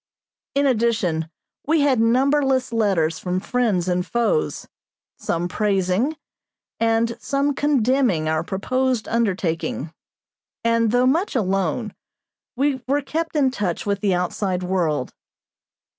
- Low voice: No, high, 225 Hz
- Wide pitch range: Yes, wide, 6.2 semitones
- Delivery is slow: Yes, slow, 115 wpm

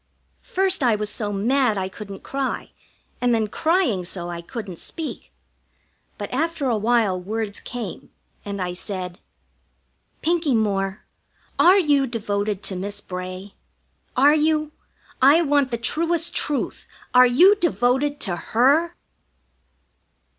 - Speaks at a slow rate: Yes, slow, 130 wpm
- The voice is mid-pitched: No, high, 235 Hz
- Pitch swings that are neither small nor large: No, wide, 6.6 semitones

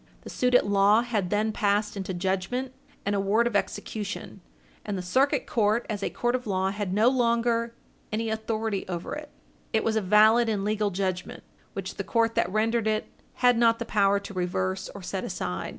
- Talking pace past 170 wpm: Yes, average, 195 wpm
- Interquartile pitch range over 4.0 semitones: No, average, 2.8 semitones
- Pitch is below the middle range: No, high, 215 Hz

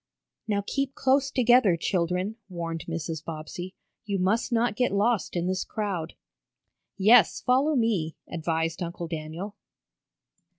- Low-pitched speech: No, high, 190 Hz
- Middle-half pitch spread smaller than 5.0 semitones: No, wide, 5.4 semitones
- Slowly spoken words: Yes, slow, 125 wpm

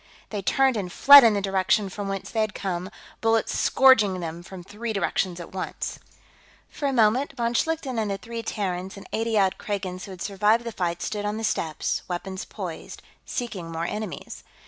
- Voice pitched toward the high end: Yes, high, 205 Hz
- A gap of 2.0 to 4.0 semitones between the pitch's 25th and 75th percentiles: Yes, average, 3.4 semitones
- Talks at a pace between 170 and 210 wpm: Yes, average, 190 wpm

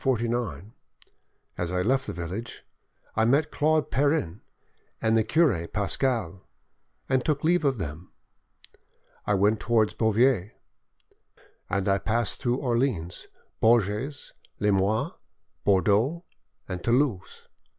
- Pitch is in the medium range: No, low, 110 Hz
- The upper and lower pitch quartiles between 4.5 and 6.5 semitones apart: Yes, wide, 5.4 semitones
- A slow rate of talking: Yes, slow, 110 wpm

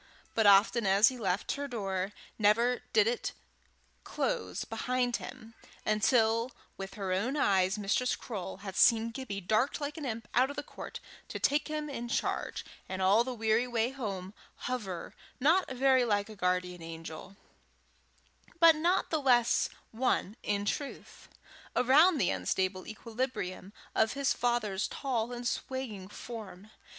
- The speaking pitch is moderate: No, high, 225 Hz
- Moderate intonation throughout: Yes, average, 4.6 semitones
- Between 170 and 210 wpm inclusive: No, average, 150 wpm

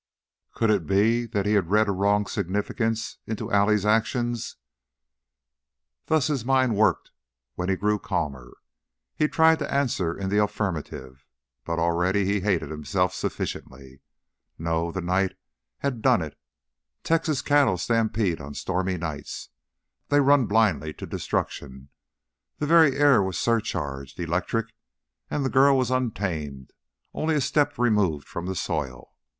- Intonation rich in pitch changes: Yes, wide, 5.9 semitones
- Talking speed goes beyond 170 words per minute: No, average, 140 wpm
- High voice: No, low, 100 Hz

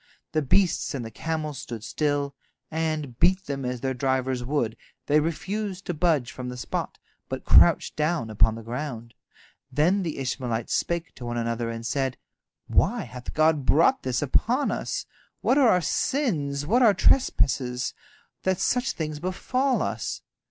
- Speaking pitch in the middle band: Yes, medium, 145 Hz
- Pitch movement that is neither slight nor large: No, wide, 5.8 semitones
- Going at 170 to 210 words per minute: No, average, 160 wpm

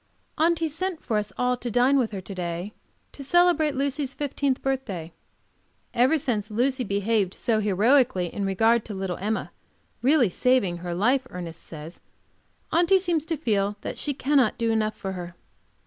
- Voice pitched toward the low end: No, high, 235 Hz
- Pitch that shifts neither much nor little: No, wide, 6.0 semitones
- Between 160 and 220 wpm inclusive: Yes, average, 165 wpm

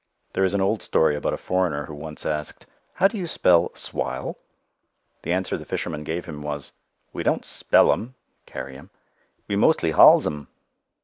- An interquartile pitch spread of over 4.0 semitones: Yes, average, 4.4 semitones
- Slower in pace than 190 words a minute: Yes, average, 175 wpm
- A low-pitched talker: Yes, very low, 80 Hz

